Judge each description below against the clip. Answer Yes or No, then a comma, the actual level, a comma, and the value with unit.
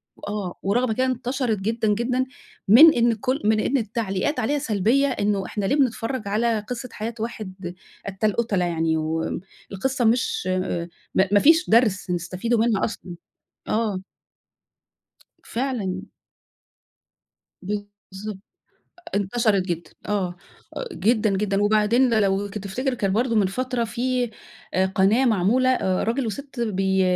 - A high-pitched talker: Yes, high, 215 Hz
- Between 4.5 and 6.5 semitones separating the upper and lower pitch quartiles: No, average, 3.9 semitones